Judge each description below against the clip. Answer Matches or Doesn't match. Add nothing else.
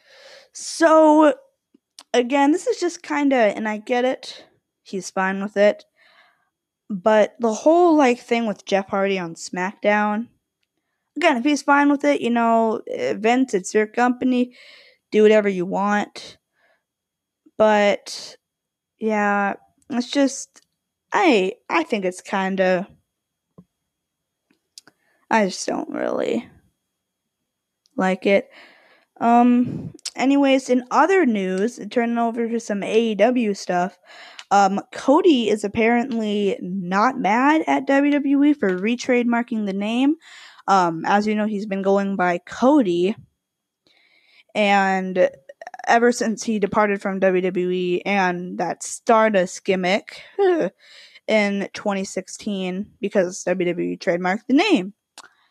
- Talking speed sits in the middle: Doesn't match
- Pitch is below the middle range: Doesn't match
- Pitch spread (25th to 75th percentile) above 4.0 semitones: Matches